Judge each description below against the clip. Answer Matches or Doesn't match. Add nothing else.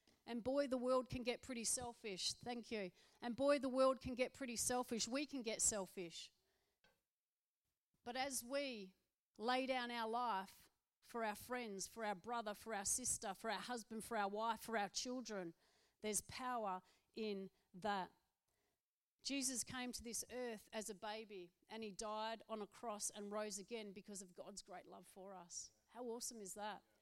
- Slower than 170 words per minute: Doesn't match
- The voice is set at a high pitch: Matches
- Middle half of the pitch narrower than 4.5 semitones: Matches